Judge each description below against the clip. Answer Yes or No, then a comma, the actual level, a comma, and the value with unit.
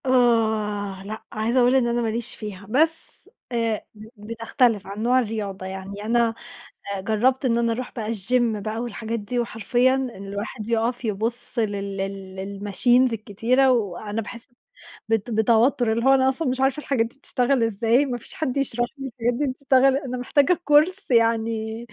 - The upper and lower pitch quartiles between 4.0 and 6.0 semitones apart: No, average, 3.0 semitones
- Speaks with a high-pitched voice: Yes, high, 230 Hz